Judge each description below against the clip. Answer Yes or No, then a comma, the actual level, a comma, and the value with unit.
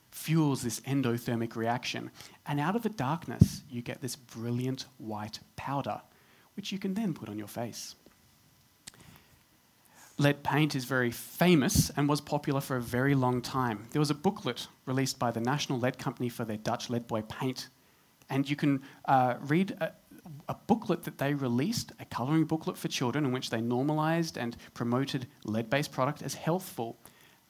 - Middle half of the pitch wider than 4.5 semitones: No, average, 3.9 semitones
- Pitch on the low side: Yes, low, 130 Hz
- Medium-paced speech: Yes, average, 170 wpm